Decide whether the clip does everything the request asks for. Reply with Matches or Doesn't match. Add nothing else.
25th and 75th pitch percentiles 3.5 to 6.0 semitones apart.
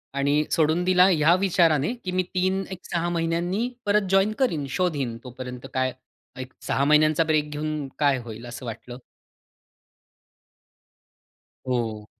Matches